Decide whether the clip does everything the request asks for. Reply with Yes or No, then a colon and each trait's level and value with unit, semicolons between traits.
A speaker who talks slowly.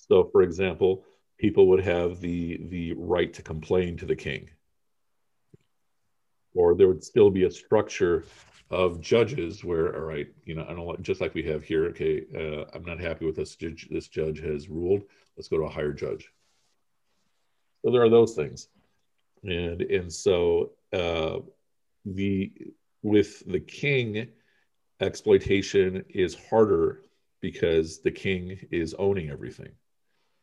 No: average, 145 wpm